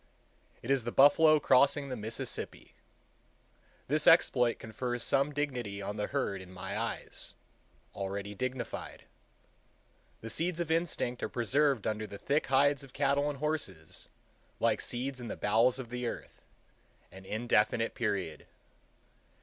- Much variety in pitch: No, average, 4.8 semitones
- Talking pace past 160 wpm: No, slow, 135 wpm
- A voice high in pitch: No, low, 125 Hz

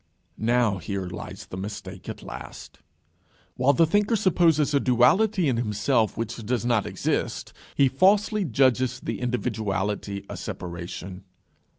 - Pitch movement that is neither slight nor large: No, wide, 5.9 semitones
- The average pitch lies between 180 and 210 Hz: No, low, 120 Hz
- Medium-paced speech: No, slow, 130 wpm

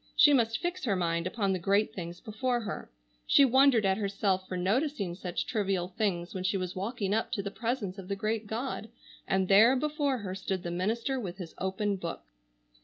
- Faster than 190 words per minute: Yes, average, 200 wpm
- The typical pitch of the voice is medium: No, high, 200 Hz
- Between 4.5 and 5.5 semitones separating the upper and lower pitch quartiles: No, average, 3.9 semitones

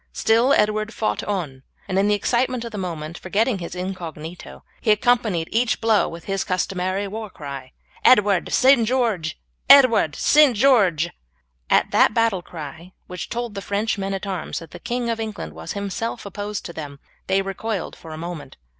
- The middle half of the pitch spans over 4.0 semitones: Yes, average, 4.7 semitones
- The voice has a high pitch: Yes, high, 200 Hz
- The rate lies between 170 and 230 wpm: Yes, average, 175 wpm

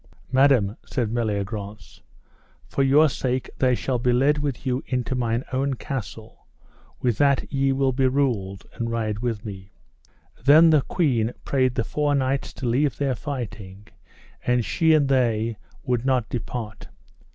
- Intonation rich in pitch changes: No, average, 3.3 semitones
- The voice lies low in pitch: Yes, low, 125 Hz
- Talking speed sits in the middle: Yes, average, 150 wpm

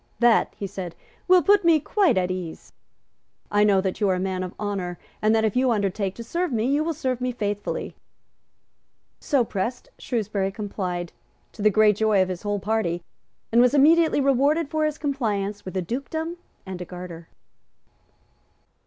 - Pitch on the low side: No, high, 215 Hz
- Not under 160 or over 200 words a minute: Yes, average, 180 wpm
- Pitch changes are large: Yes, wide, 6.1 semitones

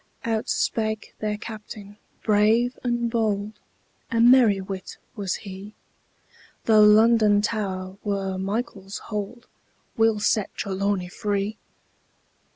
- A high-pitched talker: Yes, high, 210 Hz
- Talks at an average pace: No, slow, 105 wpm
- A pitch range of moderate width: No, narrow, 2.1 semitones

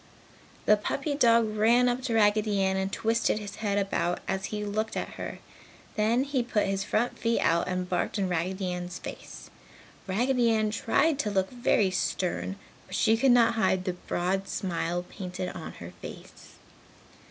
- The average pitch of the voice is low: No, high, 205 Hz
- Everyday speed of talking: Yes, average, 175 wpm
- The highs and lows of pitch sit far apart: No, average, 3.6 semitones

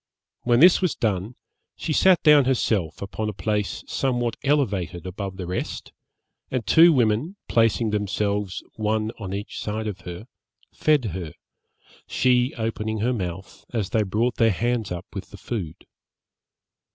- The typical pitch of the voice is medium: No, low, 110 Hz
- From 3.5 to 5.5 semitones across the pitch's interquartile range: Yes, average, 4.0 semitones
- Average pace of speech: Yes, average, 150 wpm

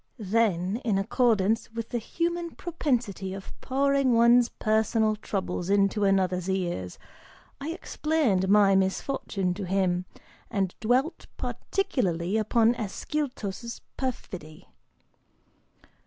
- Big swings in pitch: No, average, 4.5 semitones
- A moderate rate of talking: No, slow, 100 wpm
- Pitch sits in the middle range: No, high, 215 Hz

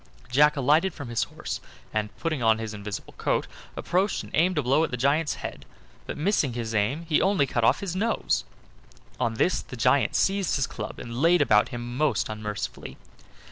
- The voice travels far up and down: Yes, wide, 6.2 semitones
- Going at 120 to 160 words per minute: No, average, 190 wpm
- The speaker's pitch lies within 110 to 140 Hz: Yes, low, 135 Hz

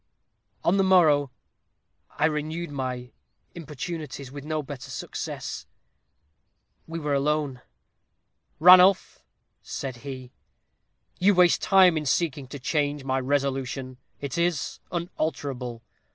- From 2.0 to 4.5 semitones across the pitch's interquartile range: Yes, average, 3.9 semitones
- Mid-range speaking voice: Yes, medium, 145 Hz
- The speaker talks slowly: Yes, slow, 110 wpm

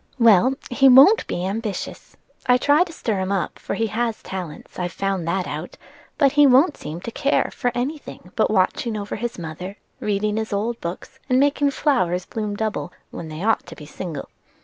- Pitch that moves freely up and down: Yes, wide, 5.8 semitones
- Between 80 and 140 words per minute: No, average, 195 wpm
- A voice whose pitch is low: No, high, 215 Hz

